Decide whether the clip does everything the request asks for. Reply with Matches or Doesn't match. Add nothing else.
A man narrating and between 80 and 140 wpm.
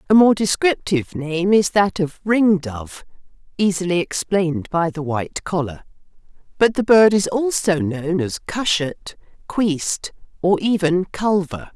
Doesn't match